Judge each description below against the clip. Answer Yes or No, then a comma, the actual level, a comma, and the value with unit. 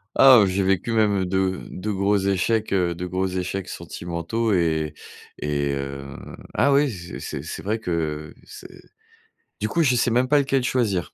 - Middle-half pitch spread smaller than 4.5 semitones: No, average, 4.8 semitones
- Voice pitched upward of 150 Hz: No, very low, 95 Hz